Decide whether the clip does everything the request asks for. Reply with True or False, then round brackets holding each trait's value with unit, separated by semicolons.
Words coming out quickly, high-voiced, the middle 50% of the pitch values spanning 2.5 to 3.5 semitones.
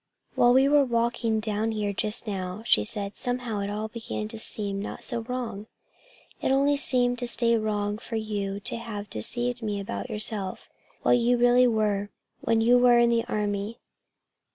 False (175 wpm; 225 Hz; 2.8 semitones)